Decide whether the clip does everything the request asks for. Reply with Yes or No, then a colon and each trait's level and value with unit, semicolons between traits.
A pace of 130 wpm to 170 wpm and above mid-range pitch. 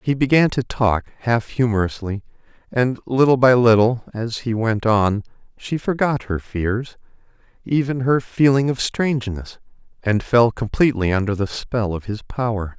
No: average, 150 wpm; low, 115 Hz